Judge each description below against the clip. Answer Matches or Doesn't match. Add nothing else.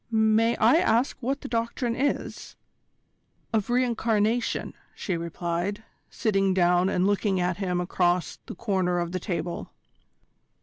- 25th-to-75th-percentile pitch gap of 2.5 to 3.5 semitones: Doesn't match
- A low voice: Doesn't match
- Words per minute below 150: Matches